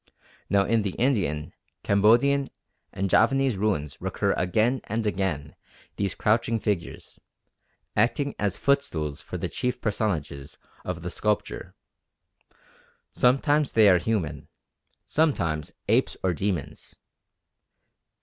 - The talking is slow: Yes, slow, 110 wpm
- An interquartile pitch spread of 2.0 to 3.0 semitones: No, wide, 5.4 semitones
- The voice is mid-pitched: No, low, 105 Hz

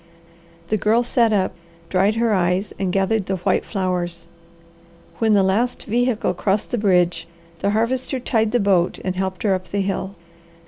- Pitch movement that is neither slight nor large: Yes, average, 3.1 semitones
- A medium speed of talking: Yes, average, 170 wpm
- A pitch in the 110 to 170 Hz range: No, high, 200 Hz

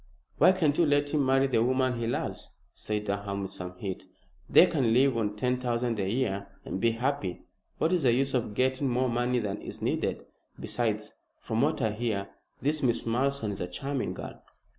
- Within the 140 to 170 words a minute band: No, average, 200 wpm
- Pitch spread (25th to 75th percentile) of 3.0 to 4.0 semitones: No, average, 4.5 semitones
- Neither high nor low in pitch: No, low, 120 Hz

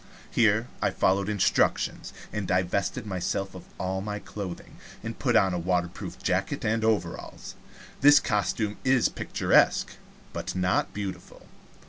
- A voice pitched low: Yes, low, 100 Hz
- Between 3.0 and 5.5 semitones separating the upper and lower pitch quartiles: No, narrow, 2.6 semitones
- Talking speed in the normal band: No, slow, 130 wpm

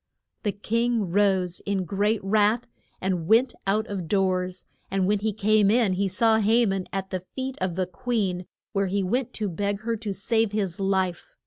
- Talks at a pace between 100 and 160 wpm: No, average, 190 wpm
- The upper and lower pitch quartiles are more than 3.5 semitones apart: No, average, 2.7 semitones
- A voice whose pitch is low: No, high, 200 Hz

